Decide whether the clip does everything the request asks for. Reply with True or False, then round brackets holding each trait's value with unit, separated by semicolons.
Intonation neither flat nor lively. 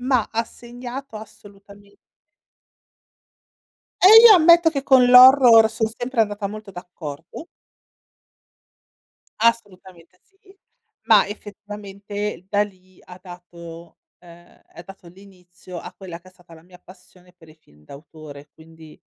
True (4.7 semitones)